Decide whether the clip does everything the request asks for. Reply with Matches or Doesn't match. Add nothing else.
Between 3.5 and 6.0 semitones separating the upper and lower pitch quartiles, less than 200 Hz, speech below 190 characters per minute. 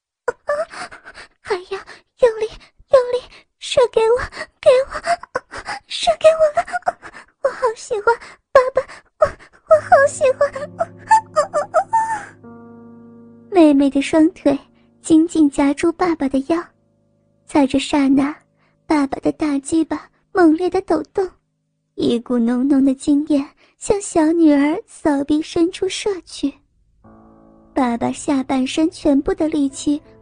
Doesn't match